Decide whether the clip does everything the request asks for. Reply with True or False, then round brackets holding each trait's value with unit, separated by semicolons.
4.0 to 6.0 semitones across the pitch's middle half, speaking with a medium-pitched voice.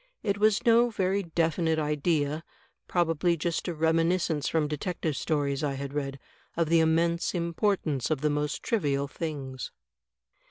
False (2.8 semitones; 160 Hz)